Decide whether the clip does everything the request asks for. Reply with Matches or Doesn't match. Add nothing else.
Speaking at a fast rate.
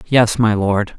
Doesn't match